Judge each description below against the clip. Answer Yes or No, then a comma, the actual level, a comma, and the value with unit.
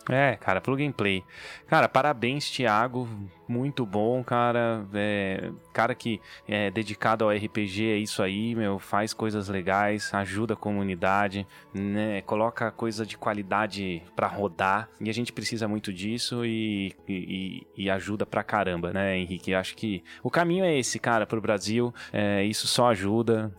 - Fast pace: No, average, 160 wpm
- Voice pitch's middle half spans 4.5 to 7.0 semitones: No, average, 2.7 semitones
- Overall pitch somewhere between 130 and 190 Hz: No, low, 105 Hz